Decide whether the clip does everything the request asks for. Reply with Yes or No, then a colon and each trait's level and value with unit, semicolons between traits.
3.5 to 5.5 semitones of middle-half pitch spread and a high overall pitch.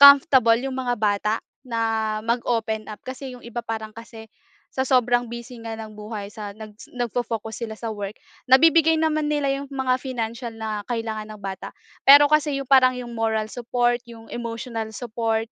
No: average, 2.8 semitones; high, 235 Hz